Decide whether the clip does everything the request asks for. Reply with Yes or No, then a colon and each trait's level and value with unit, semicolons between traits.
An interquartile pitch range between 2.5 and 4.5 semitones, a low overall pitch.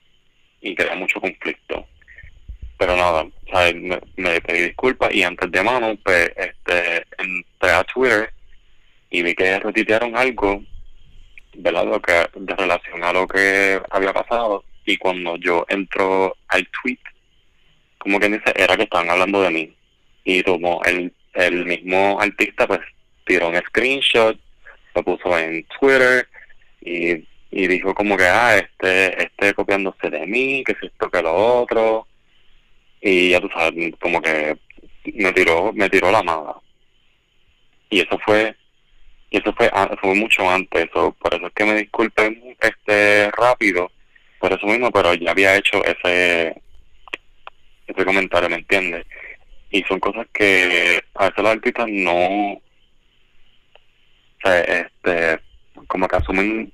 Yes: average, 3.1 semitones; very low, 95 Hz